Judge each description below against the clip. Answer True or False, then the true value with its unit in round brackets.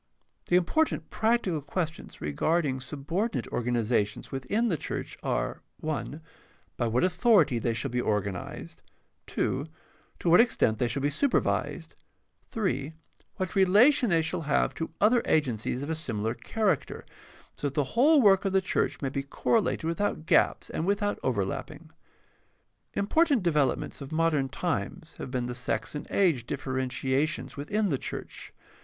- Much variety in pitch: True (6.8 semitones)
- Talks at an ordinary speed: True (150 wpm)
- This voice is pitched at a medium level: True (155 Hz)